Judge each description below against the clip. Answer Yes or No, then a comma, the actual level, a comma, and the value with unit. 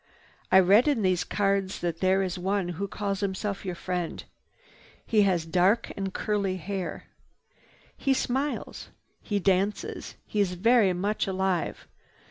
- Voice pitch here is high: Yes, high, 195 Hz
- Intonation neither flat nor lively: No, narrow, 2.0 semitones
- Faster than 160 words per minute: No, average, 140 wpm